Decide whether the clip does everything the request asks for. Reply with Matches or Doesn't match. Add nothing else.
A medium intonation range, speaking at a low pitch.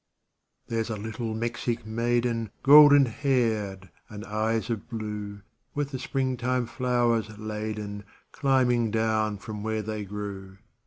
Doesn't match